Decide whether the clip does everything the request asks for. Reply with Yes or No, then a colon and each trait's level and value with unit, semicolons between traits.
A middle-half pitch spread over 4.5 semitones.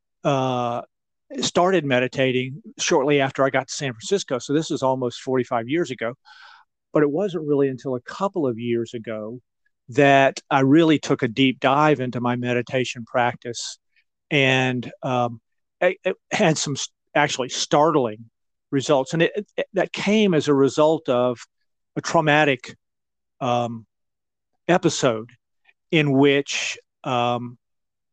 No: average, 3.9 semitones